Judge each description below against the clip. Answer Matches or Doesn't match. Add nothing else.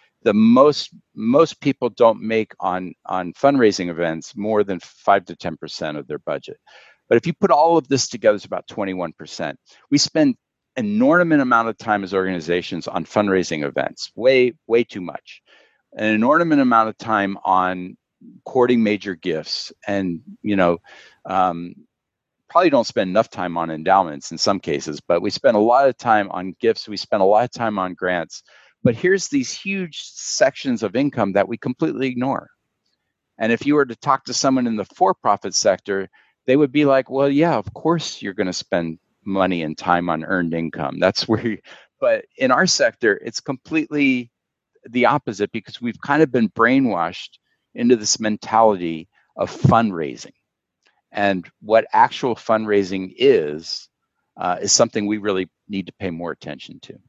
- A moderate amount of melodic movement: Doesn't match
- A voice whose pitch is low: Matches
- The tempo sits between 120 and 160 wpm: Doesn't match